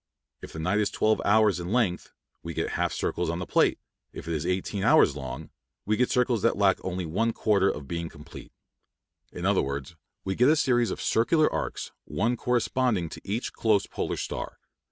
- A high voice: No, low, 100 Hz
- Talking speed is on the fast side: No, average, 195 wpm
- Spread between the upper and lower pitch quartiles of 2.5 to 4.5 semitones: No, average, 5.2 semitones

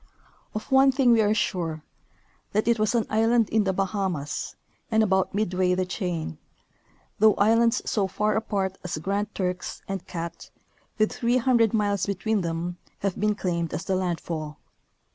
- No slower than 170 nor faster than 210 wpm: No, average, 160 wpm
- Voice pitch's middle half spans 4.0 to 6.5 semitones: No, average, 3.3 semitones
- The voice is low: No, high, 200 Hz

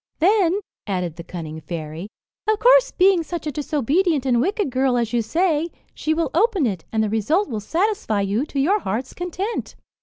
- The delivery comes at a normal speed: Yes, average, 185 wpm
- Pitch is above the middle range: Yes, very high, 290 Hz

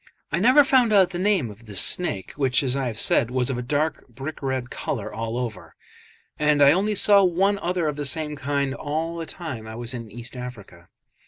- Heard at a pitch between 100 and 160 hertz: Yes, medium, 140 Hz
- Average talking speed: No, fast, 220 wpm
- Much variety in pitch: Yes, wide, 6.0 semitones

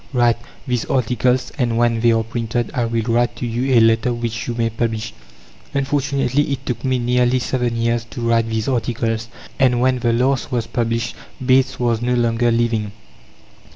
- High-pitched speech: No, low, 120 Hz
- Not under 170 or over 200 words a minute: Yes, average, 180 wpm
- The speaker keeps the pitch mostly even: Yes, narrow, 1.4 semitones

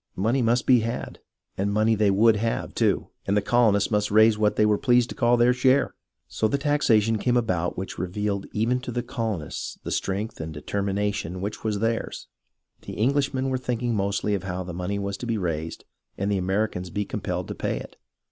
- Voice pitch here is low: Yes, low, 105 Hz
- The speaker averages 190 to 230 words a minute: Yes, fast, 205 wpm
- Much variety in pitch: No, average, 3.3 semitones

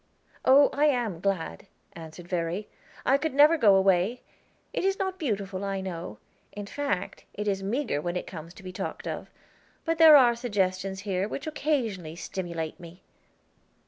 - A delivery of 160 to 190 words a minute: Yes, average, 165 wpm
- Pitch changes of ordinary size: No, wide, 6.7 semitones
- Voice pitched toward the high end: Yes, high, 195 Hz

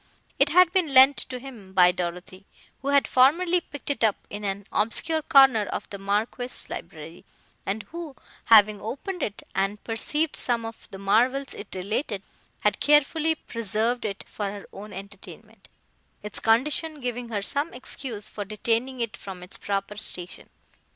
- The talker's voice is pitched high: Yes, high, 225 Hz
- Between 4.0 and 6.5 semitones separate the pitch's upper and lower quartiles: Yes, wide, 5.4 semitones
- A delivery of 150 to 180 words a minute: Yes, average, 160 wpm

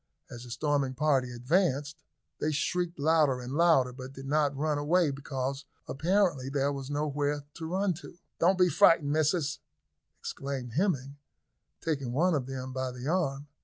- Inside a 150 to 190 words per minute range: Yes, average, 165 wpm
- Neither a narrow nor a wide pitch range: Yes, average, 3.2 semitones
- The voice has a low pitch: No, medium, 145 Hz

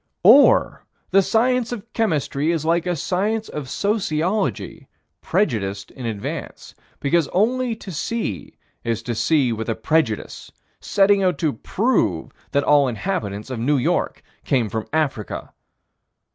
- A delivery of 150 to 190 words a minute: No, slow, 135 wpm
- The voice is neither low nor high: Yes, medium, 155 Hz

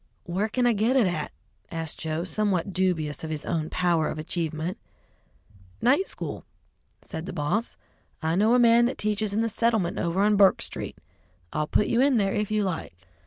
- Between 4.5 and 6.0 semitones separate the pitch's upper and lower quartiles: Yes, average, 5.1 semitones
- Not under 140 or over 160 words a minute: No, average, 190 wpm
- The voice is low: No, high, 190 Hz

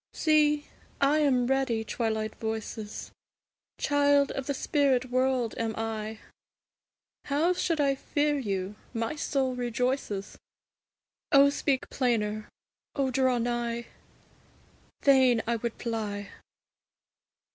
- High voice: Yes, very high, 250 Hz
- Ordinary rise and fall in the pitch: Yes, average, 3.9 semitones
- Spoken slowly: Yes, slow, 105 wpm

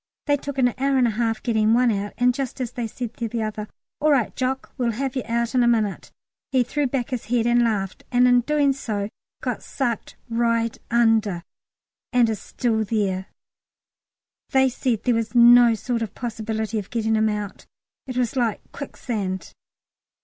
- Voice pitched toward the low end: No, high, 235 Hz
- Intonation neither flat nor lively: No, narrow, 2.3 semitones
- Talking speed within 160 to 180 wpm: No, average, 190 wpm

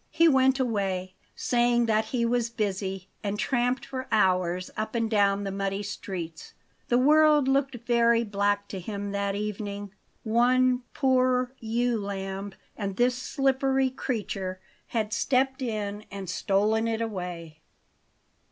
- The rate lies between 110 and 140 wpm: Yes, slow, 135 wpm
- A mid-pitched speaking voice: No, high, 220 Hz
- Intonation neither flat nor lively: Yes, average, 4.0 semitones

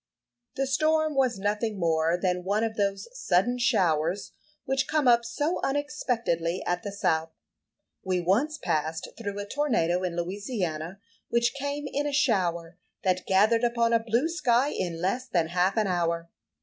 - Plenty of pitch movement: Yes, wide, 6.4 semitones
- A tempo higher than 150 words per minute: Yes, average, 160 wpm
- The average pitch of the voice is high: Yes, high, 205 Hz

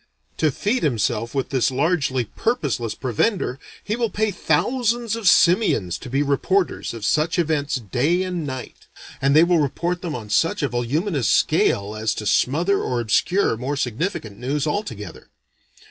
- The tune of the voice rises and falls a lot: Yes, wide, 6.7 semitones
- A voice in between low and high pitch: Yes, medium, 145 Hz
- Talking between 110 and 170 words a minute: Yes, average, 160 wpm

